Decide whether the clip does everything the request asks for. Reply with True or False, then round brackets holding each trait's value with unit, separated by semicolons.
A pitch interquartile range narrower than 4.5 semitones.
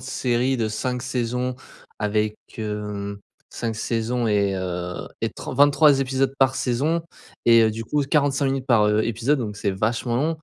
True (3.8 semitones)